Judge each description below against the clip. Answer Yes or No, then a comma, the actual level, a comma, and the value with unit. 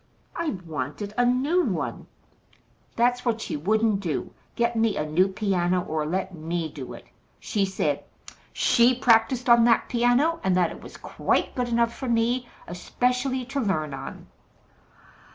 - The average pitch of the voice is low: No, high, 225 Hz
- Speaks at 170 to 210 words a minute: No, average, 155 wpm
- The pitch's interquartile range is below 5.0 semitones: No, wide, 5.5 semitones